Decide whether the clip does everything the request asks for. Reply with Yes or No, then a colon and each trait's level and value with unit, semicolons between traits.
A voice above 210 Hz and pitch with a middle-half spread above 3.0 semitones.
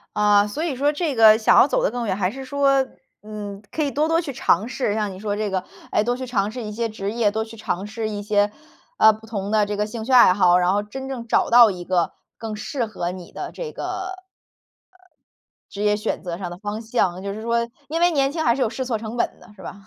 Yes: high, 220 Hz; average, 4.0 semitones